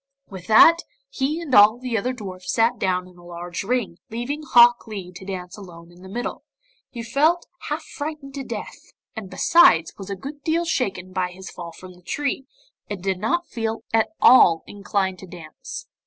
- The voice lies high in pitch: Yes, high, 210 Hz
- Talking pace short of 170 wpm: No, average, 190 wpm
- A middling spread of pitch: No, wide, 6.4 semitones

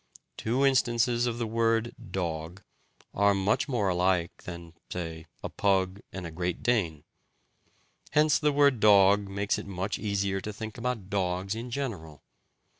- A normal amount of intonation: Yes, average, 4.3 semitones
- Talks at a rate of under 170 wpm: Yes, average, 150 wpm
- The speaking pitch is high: No, low, 100 Hz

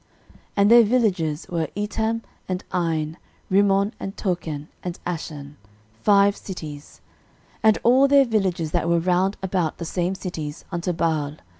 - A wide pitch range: No, average, 3.9 semitones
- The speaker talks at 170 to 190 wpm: No, average, 150 wpm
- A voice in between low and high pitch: Yes, medium, 180 Hz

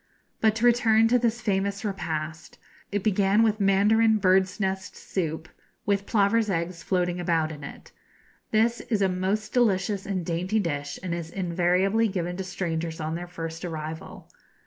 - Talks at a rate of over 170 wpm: No, average, 160 wpm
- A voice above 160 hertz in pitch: Yes, high, 190 Hz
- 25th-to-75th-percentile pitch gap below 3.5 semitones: No, average, 3.9 semitones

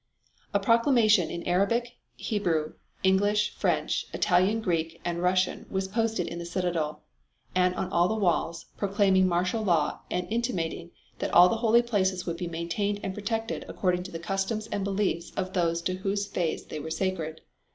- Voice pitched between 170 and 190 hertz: Yes, medium, 185 Hz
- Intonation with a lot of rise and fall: No, average, 3.2 semitones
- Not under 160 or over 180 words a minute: Yes, average, 170 wpm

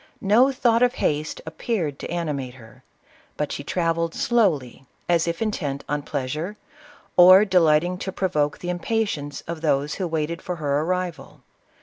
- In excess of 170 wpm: No, average, 150 wpm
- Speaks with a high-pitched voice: No, medium, 165 Hz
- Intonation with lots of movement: No, average, 4.0 semitones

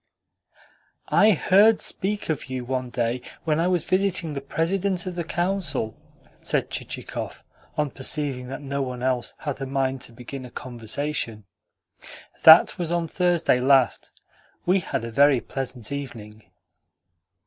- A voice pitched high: No, medium, 140 Hz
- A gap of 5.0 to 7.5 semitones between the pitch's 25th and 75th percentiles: Yes, wide, 5.4 semitones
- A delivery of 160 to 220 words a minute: No, average, 145 wpm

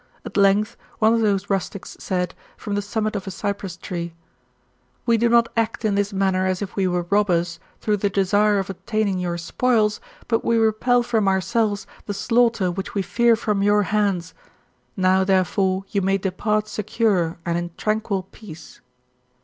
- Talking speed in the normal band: Yes, average, 175 wpm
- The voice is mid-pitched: No, high, 200 Hz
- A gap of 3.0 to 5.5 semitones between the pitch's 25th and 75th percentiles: No, narrow, 2.4 semitones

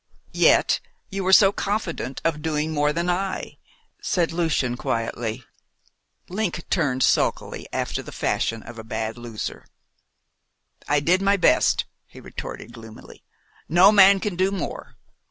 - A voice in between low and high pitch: Yes, medium, 165 Hz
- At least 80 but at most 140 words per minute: Yes, slow, 135 wpm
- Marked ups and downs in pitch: Yes, wide, 7.7 semitones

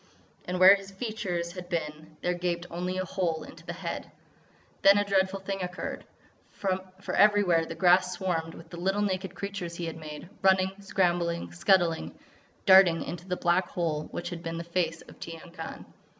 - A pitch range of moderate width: No, narrow, 2.1 semitones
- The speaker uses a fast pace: No, average, 180 wpm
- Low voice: No, medium, 180 Hz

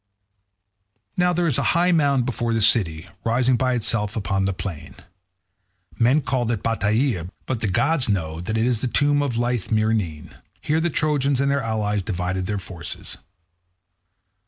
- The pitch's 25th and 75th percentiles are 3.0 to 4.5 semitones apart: No, wide, 5.5 semitones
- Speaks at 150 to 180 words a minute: Yes, average, 165 wpm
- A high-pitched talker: No, low, 115 Hz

